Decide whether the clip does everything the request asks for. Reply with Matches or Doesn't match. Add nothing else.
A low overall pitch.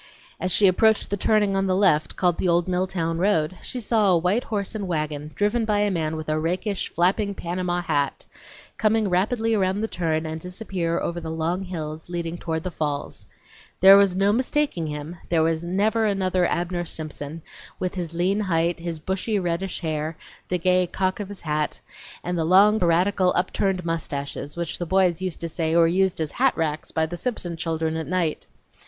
Doesn't match